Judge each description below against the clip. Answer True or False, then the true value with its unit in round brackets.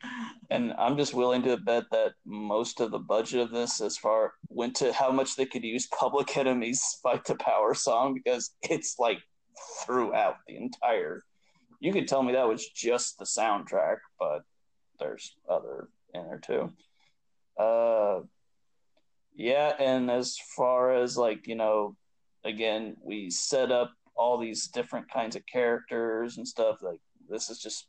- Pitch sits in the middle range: False (125 Hz)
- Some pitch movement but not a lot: True (3.1 semitones)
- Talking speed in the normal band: True (160 wpm)